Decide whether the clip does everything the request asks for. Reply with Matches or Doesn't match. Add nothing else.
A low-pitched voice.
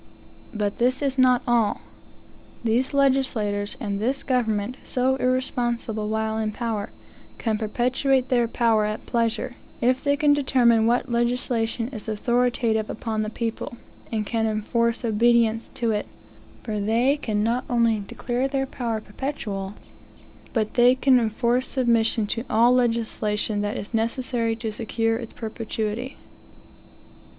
Doesn't match